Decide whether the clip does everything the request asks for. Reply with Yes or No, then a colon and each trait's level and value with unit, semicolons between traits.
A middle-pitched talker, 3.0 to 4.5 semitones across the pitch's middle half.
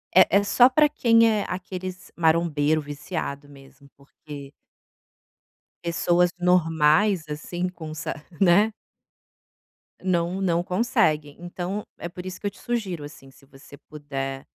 Yes: medium, 175 Hz; average, 4.2 semitones